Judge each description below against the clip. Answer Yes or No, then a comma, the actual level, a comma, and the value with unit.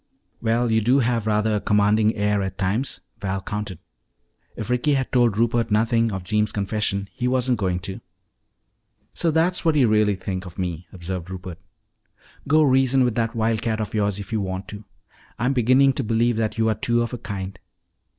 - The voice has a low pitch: Yes, low, 110 Hz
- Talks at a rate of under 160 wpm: No, average, 190 wpm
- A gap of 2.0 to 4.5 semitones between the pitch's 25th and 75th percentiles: Yes, average, 3.3 semitones